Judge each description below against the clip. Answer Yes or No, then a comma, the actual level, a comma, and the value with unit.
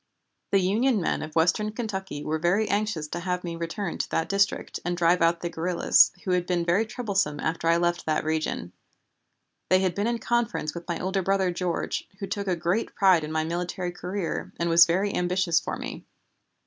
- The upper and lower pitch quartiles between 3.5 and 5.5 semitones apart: No, average, 2.7 semitones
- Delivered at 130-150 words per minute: No, fast, 205 wpm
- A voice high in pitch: No, medium, 180 Hz